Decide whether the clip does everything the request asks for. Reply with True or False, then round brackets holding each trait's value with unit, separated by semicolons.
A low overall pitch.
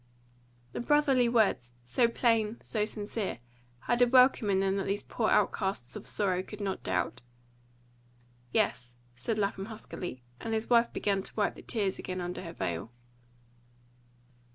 False (205 Hz)